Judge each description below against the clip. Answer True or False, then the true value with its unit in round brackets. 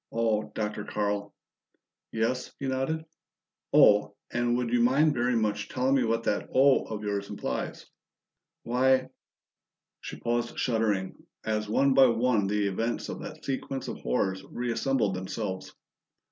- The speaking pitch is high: False (115 Hz)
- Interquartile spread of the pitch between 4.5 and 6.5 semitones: False (3.5 semitones)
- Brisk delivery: False (145 wpm)